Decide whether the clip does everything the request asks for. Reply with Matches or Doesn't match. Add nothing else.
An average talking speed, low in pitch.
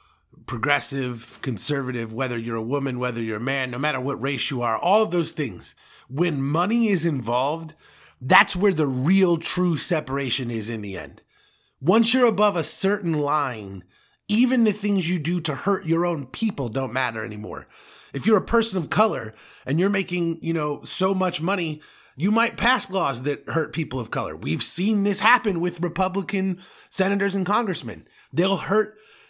Doesn't match